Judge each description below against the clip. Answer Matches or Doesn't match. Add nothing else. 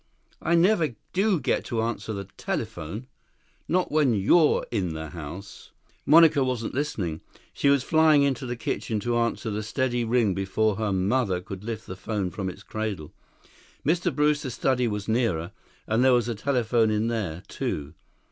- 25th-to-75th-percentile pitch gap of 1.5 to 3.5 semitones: Doesn't match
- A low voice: Matches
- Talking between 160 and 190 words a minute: Matches